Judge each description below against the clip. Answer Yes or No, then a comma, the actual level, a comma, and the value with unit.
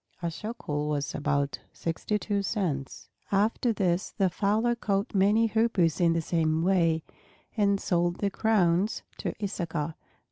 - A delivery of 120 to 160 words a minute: Yes, average, 140 wpm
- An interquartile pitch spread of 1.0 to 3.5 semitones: No, average, 4.2 semitones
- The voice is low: No, medium, 185 Hz